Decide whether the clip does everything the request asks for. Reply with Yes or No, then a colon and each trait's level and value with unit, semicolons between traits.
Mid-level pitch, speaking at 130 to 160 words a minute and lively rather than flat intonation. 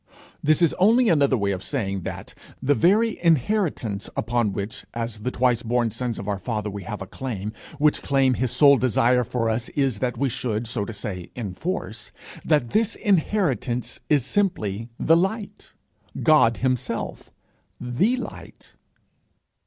No: low, 125 Hz; average, 155 wpm; wide, 5.8 semitones